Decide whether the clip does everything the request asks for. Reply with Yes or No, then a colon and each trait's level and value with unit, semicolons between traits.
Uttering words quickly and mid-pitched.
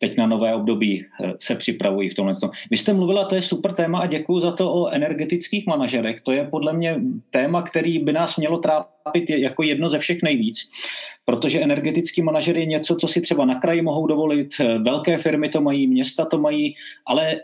Yes: fast, 195 wpm; medium, 160 Hz